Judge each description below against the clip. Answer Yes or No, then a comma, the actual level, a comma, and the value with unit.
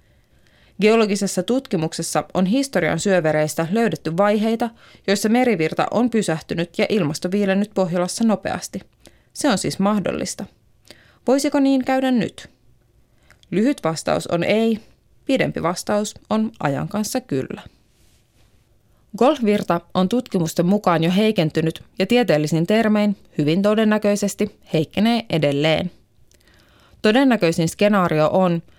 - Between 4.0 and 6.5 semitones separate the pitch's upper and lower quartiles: Yes, average, 5.1 semitones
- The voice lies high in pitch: Yes, high, 195 Hz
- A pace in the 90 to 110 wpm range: Yes, average, 105 wpm